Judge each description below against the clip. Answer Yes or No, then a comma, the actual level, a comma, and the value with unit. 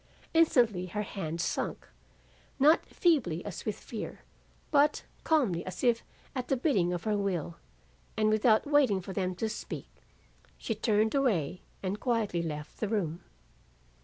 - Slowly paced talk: No, average, 145 wpm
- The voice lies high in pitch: Yes, high, 210 Hz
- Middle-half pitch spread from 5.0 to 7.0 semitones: Yes, wide, 5.4 semitones